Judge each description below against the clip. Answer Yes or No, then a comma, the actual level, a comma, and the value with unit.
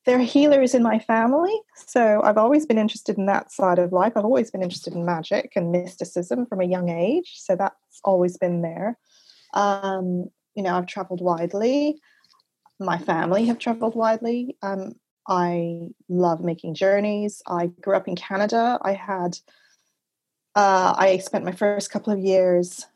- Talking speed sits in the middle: Yes, average, 165 wpm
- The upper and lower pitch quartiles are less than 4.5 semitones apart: Yes, average, 4.0 semitones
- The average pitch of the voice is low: No, high, 195 Hz